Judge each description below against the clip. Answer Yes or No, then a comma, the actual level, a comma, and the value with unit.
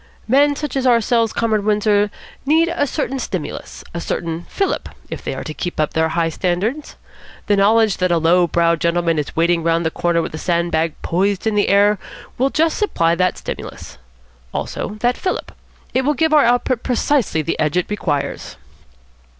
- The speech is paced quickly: No, average, 185 wpm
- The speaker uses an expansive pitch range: Yes, wide, 6.8 semitones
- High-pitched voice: Yes, high, 200 Hz